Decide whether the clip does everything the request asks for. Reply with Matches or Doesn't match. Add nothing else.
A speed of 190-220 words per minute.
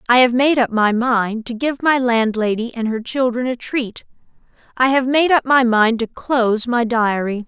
Matches